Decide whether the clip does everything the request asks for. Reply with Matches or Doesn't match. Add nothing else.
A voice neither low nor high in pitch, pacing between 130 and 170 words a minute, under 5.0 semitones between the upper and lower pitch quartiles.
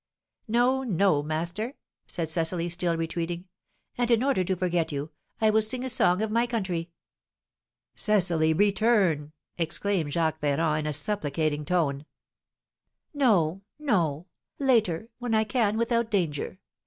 Doesn't match